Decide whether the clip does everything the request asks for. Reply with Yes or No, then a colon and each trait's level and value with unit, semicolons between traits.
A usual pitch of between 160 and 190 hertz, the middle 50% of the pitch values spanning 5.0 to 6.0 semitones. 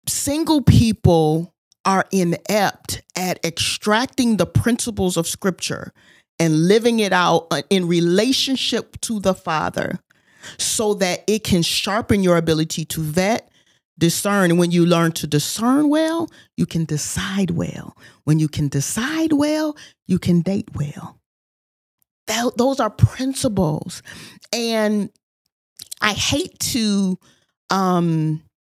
Yes: medium, 185 Hz; average, 5.3 semitones